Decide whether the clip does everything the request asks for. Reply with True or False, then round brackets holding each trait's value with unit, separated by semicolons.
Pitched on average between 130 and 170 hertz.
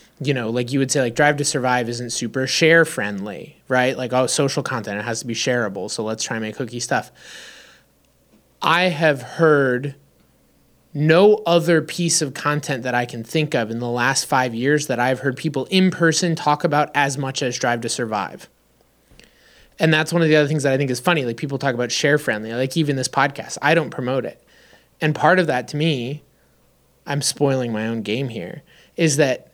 True (135 Hz)